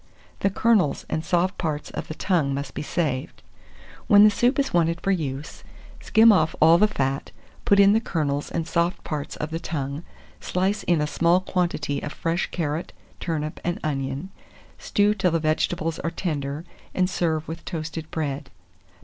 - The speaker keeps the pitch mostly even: No, average, 3.6 semitones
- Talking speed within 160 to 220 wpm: Yes, average, 175 wpm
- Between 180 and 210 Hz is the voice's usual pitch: No, medium, 165 Hz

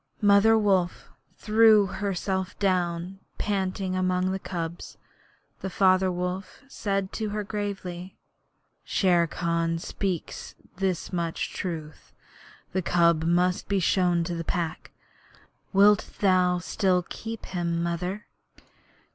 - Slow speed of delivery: Yes, slow, 115 wpm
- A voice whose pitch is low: No, medium, 185 Hz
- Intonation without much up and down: Yes, narrow, 2.3 semitones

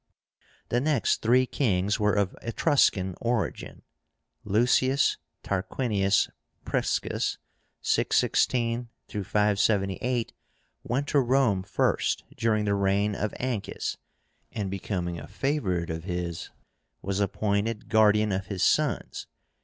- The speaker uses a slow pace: Yes, slow, 105 wpm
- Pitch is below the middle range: Yes, low, 105 Hz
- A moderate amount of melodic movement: Yes, average, 3.6 semitones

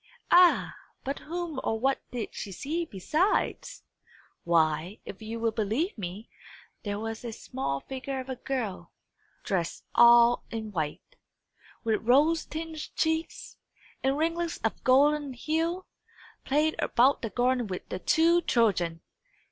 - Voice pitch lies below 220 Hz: No, very high, 250 Hz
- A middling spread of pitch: No, wide, 6.3 semitones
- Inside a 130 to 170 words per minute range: Yes, slow, 135 wpm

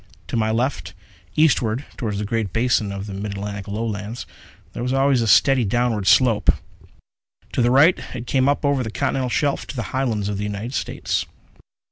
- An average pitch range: Yes, average, 3.9 semitones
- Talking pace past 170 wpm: Yes, average, 185 wpm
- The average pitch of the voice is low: Yes, low, 115 Hz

